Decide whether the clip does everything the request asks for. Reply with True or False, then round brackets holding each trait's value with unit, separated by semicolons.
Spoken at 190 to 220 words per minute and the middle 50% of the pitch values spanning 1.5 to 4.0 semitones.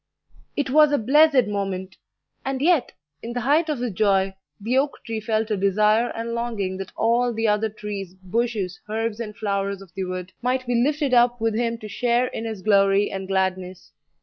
True (195 wpm; 3.7 semitones)